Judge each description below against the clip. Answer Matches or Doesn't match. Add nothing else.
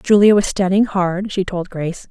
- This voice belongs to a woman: Matches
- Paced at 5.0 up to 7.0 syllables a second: Doesn't match